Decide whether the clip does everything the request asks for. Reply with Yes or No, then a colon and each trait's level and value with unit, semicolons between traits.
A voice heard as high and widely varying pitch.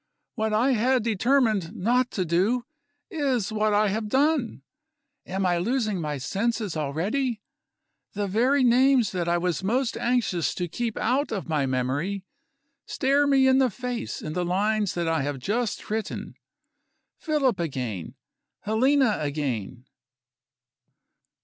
Yes: high, 215 Hz; wide, 6.3 semitones